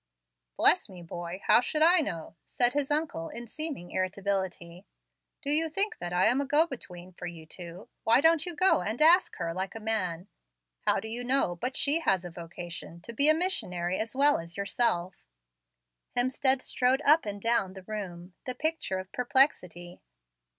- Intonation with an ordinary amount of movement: No, wide, 8.1 semitones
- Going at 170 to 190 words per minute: Yes, average, 185 wpm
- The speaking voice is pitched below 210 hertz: No, high, 215 Hz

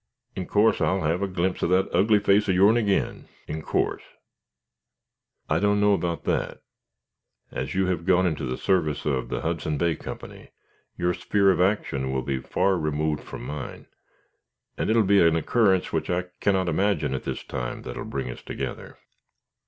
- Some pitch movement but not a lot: Yes, average, 4.3 semitones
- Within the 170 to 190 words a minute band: Yes, average, 185 wpm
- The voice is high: No, very low, 90 Hz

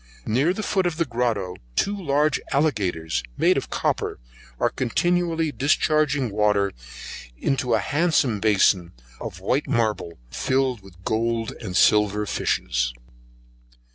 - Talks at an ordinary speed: No, slow, 125 wpm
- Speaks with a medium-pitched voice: No, low, 115 Hz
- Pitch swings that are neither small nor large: No, wide, 6.8 semitones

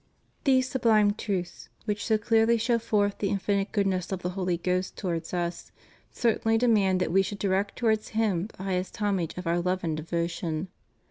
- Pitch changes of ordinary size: Yes, average, 3.2 semitones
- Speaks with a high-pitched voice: Yes, high, 195 Hz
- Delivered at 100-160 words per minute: No, average, 185 wpm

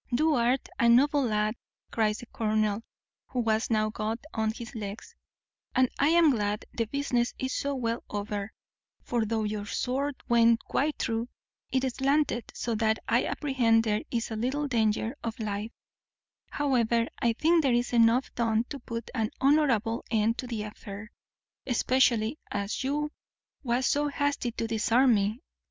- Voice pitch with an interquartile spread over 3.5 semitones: No, average, 3.2 semitones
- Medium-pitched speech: No, high, 235 Hz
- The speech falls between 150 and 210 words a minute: Yes, average, 160 wpm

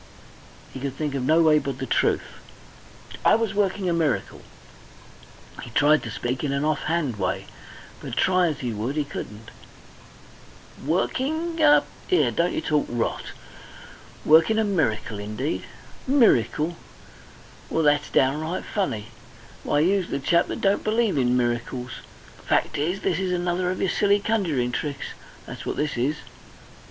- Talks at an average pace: Yes, average, 155 wpm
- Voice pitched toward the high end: No, medium, 155 Hz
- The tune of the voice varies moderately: No, wide, 6.1 semitones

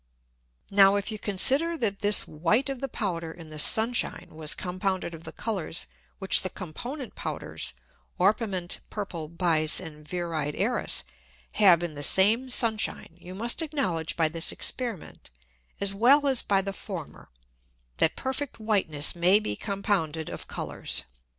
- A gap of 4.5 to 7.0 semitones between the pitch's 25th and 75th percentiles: Yes, average, 5.1 semitones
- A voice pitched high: Yes, high, 195 Hz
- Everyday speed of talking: Yes, average, 155 wpm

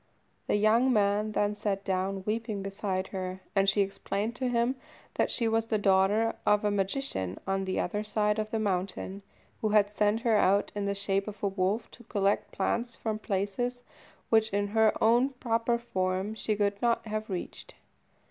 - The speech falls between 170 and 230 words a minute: Yes, average, 185 wpm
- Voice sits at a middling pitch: No, high, 210 Hz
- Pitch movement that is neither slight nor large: No, narrow, 2.2 semitones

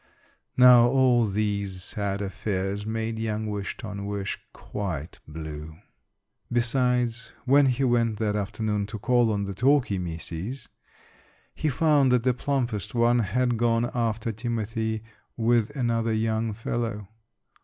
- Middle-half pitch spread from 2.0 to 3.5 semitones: Yes, average, 2.9 semitones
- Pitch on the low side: Yes, low, 110 Hz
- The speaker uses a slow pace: Yes, slow, 130 wpm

